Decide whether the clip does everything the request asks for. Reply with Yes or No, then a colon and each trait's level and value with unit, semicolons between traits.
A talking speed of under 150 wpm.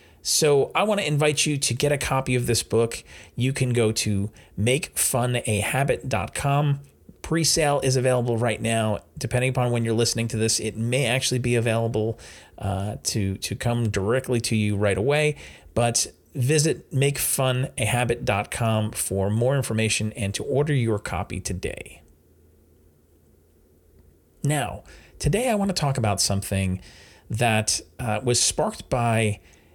Yes: average, 140 wpm